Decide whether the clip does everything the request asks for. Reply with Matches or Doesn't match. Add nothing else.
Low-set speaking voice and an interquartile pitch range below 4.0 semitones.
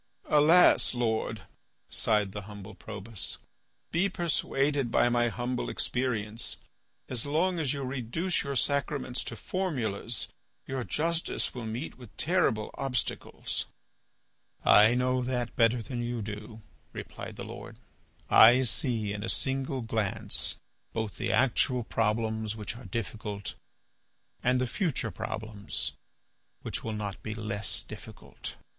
Matches